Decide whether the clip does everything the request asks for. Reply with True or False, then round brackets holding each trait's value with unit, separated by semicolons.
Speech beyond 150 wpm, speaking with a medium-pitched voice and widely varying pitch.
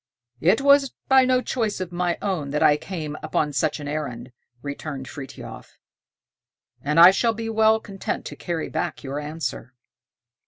True (160 wpm; 165 Hz; 7.0 semitones)